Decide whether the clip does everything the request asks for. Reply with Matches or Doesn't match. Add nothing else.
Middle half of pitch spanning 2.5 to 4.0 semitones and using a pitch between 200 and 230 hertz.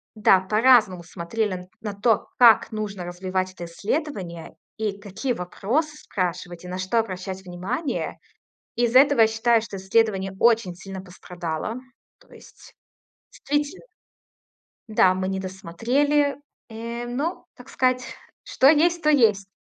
Doesn't match